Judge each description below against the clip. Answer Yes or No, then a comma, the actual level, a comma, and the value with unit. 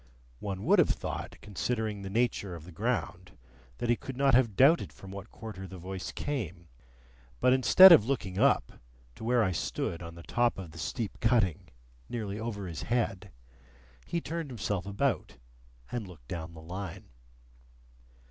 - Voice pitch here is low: Yes, low, 100 Hz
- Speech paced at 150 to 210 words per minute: Yes, average, 165 wpm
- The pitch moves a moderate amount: Yes, average, 4.9 semitones